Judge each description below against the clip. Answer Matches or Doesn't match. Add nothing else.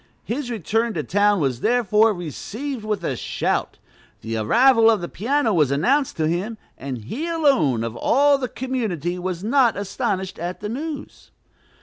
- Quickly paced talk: Doesn't match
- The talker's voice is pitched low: Doesn't match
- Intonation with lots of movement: Matches